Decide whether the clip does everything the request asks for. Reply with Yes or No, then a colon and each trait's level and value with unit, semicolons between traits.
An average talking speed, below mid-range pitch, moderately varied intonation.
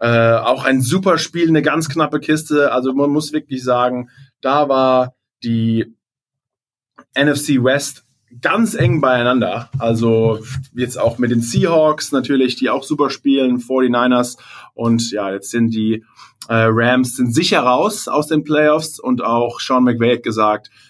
Yes: average, 150 wpm; low, 130 Hz; average, 3.4 semitones